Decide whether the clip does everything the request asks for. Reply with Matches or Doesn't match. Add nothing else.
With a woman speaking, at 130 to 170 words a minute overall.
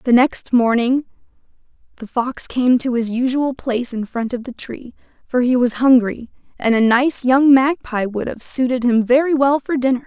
Doesn't match